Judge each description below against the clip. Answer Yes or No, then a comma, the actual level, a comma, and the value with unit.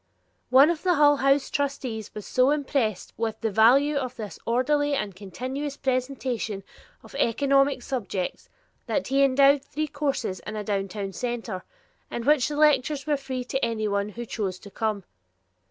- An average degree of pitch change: Yes, average, 4.5 semitones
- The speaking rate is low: No, average, 160 wpm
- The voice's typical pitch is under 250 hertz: No, very high, 255 Hz